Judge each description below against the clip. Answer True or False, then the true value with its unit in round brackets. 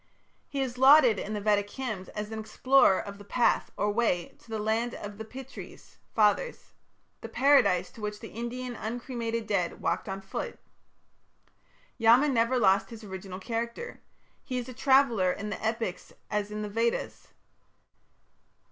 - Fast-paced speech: False (160 wpm)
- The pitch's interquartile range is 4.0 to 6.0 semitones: False (3.2 semitones)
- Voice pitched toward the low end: False (220 Hz)